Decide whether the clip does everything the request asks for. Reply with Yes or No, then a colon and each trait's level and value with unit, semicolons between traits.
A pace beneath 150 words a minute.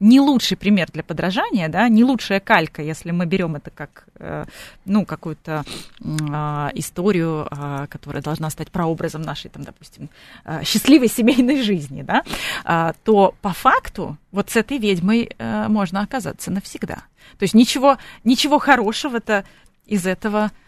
Yes: average, 135 wpm